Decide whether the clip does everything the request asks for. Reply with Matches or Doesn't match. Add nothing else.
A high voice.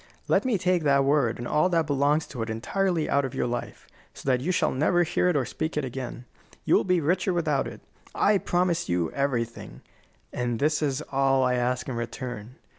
Doesn't match